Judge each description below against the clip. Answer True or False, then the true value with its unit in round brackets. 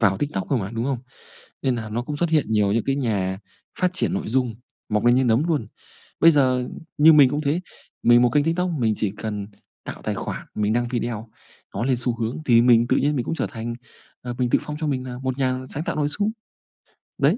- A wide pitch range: False (4.3 semitones)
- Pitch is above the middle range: False (125 Hz)